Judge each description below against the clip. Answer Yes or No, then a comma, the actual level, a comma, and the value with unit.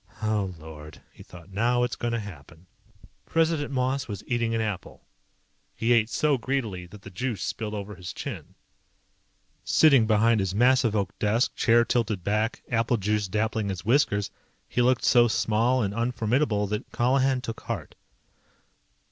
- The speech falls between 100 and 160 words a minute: Yes, average, 155 wpm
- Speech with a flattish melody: No, average, 3.2 semitones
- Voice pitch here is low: Yes, low, 110 Hz